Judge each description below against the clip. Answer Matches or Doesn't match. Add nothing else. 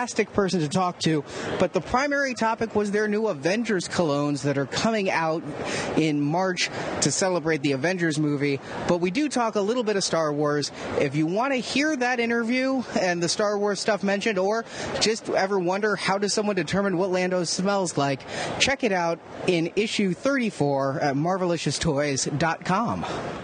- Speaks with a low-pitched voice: Doesn't match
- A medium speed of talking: Matches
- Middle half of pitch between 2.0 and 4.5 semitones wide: Doesn't match